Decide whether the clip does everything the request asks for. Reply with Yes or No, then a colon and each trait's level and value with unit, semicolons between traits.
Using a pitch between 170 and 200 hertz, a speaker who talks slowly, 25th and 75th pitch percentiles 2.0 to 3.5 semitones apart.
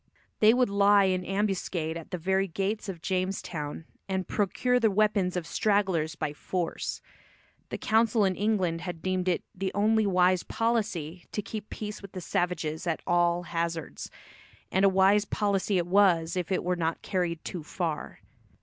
No: medium, 185 Hz; average, 170 wpm; average, 2.9 semitones